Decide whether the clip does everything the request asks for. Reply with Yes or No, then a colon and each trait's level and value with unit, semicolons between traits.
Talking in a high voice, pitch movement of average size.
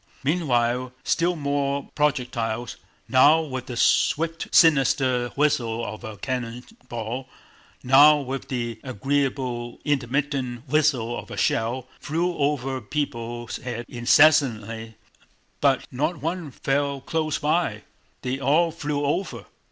No: low, 135 Hz; average, 3.5 semitones